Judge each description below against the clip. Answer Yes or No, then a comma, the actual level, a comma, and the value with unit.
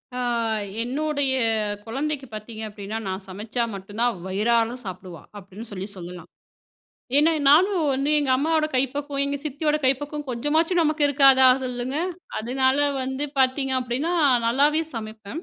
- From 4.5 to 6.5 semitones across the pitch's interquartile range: Yes, average, 4.8 semitones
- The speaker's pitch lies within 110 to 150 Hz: No, very high, 260 Hz